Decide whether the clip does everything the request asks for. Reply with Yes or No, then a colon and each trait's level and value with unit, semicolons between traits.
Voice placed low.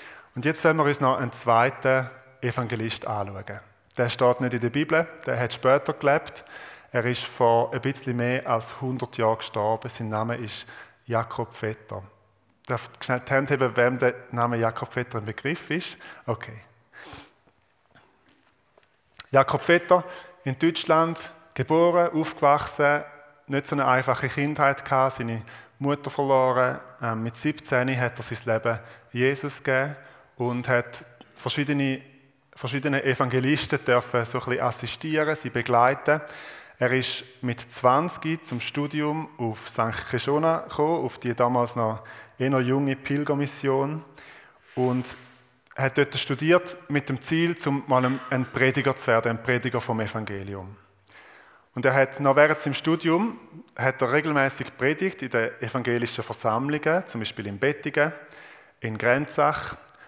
Yes: low, 130 Hz